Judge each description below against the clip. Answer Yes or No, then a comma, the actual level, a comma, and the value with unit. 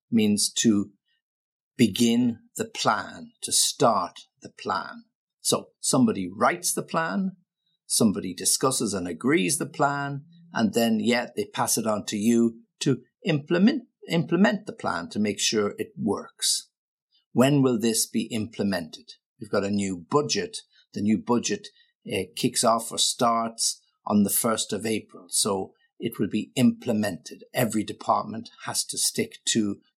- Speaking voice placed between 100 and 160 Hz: Yes, low, 135 Hz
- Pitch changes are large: Yes, wide, 8.9 semitones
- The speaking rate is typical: Yes, average, 150 wpm